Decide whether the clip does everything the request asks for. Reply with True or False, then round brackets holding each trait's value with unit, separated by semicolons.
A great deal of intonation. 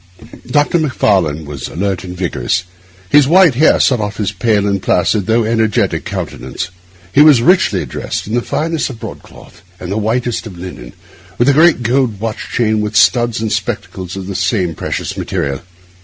False (4.8 semitones)